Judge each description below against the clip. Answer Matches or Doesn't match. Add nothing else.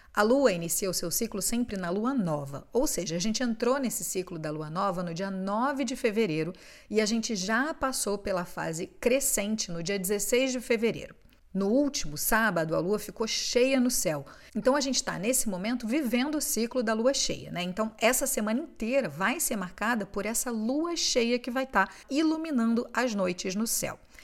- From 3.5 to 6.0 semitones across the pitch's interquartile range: Matches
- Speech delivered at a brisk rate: Matches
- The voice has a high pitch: Matches